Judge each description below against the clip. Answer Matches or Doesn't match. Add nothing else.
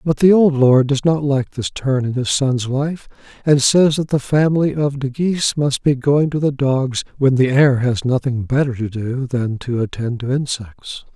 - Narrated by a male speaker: Matches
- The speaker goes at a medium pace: Doesn't match